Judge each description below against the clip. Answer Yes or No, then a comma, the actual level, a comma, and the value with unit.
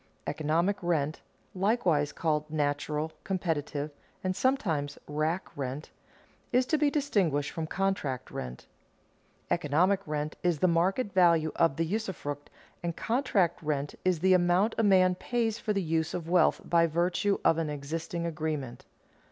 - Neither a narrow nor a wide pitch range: Yes, average, 3.9 semitones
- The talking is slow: No, average, 145 wpm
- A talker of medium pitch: Yes, medium, 170 Hz